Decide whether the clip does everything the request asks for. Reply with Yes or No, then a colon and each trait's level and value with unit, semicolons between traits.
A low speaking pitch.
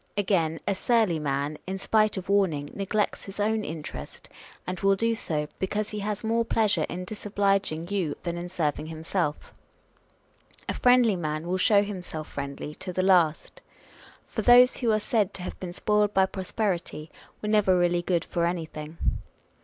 No: high, 190 Hz